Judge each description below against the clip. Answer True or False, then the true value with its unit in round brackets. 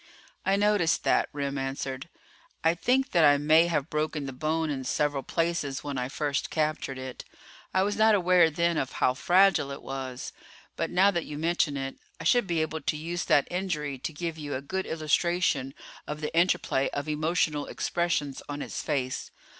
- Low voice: False (155 Hz)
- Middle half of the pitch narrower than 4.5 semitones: True (3.7 semitones)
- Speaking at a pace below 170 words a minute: False (185 wpm)